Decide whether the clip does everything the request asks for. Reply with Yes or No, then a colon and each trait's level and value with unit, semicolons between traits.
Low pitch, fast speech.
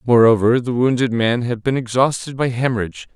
No: low, 120 Hz; average, 170 wpm